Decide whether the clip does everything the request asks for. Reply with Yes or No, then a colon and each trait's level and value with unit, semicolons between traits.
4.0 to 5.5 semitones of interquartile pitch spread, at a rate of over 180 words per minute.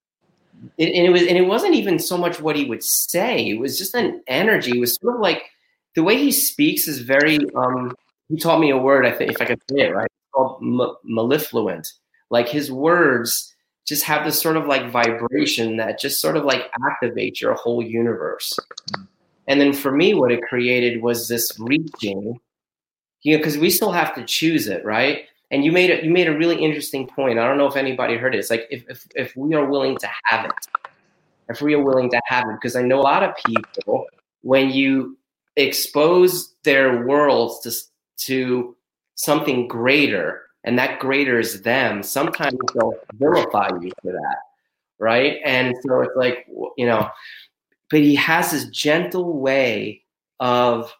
Yes: average, 4.6 semitones; average, 190 wpm